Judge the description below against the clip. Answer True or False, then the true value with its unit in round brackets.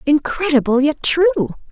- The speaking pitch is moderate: False (310 Hz)